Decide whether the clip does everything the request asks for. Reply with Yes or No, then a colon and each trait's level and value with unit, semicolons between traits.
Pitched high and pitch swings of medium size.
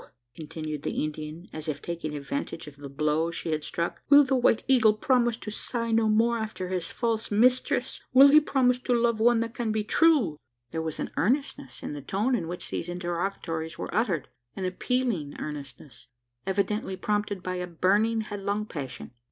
No: high, 200 Hz; wide, 6.5 semitones